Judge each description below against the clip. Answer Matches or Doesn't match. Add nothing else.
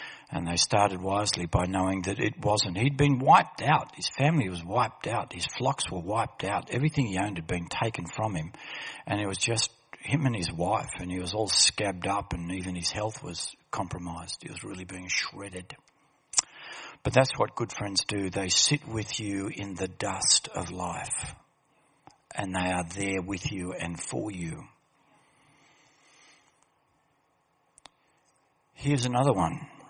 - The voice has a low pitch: Matches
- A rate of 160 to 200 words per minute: Matches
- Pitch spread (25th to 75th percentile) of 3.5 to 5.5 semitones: Matches